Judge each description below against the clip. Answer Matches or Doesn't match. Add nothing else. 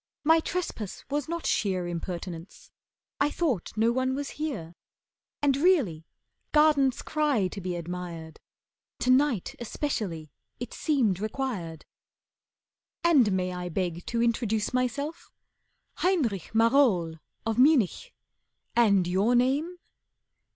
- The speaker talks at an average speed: Doesn't match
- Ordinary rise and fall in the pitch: Doesn't match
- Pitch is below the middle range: Doesn't match